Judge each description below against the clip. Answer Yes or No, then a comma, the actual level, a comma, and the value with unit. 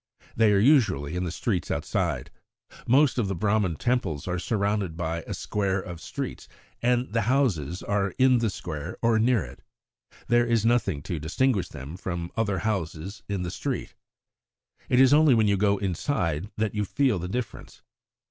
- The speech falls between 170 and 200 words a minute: Yes, average, 175 wpm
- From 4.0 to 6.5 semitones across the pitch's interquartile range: Yes, average, 5.0 semitones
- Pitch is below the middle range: Yes, low, 100 Hz